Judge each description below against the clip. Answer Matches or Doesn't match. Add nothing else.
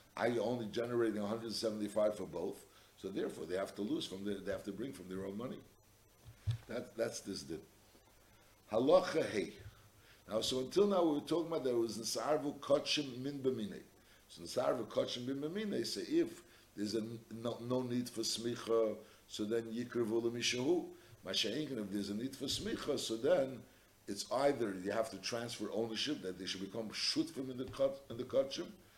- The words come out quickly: Doesn't match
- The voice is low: Matches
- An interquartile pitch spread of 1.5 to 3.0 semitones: Doesn't match